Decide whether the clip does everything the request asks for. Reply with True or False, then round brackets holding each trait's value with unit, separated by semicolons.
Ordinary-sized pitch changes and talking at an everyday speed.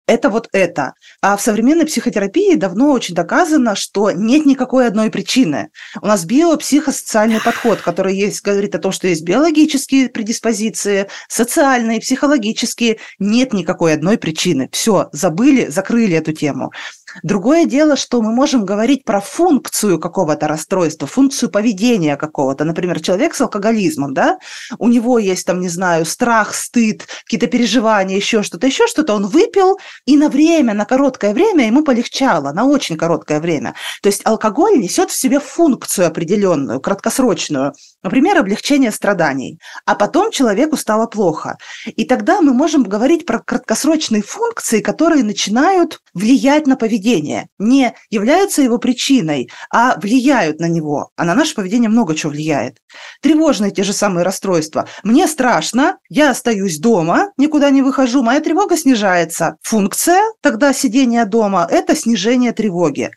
False (5.9 semitones; 145 wpm)